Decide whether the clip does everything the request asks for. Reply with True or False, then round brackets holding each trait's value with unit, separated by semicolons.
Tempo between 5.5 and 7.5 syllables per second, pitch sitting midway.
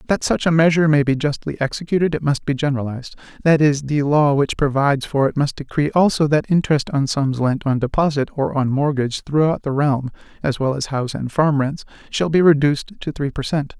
True (5.8 syllables/s; 145 Hz)